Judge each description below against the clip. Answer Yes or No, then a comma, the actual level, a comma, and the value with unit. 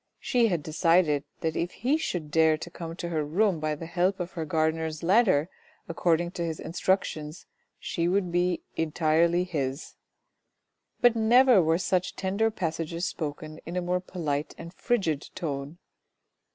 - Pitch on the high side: No, medium, 170 Hz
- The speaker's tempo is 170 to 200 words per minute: No, average, 160 wpm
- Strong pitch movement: No, narrow, 2.6 semitones